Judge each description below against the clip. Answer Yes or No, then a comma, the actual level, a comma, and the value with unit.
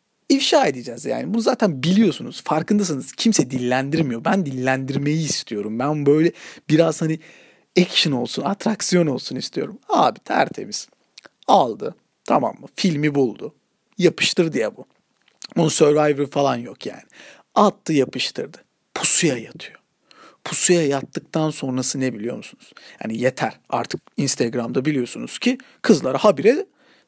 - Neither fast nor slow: Yes, average, 120 wpm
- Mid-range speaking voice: Yes, medium, 155 Hz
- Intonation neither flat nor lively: No, wide, 6.1 semitones